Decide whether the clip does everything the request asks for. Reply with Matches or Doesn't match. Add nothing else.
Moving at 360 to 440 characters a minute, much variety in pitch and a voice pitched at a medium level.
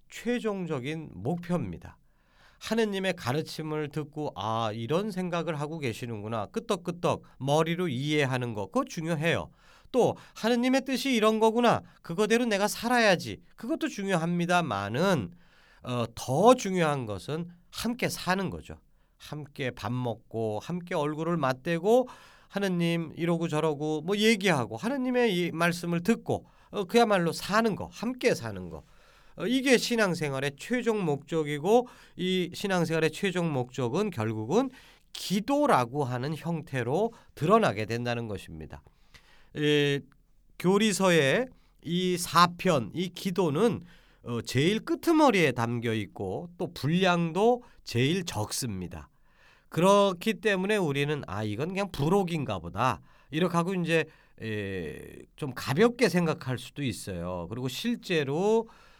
Doesn't match